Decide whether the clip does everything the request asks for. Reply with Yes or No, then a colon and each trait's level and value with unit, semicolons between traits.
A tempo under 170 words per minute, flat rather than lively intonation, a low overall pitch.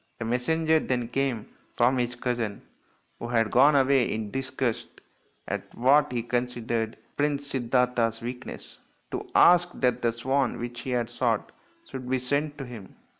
Yes: average, 155 wpm; narrow, 2.3 semitones; low, 125 Hz